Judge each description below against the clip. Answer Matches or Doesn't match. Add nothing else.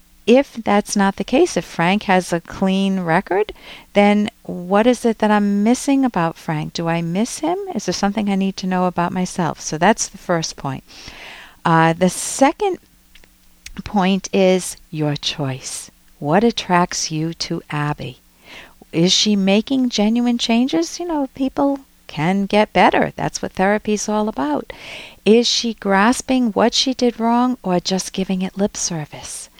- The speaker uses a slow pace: Doesn't match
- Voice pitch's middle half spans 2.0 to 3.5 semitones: Doesn't match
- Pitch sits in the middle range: Doesn't match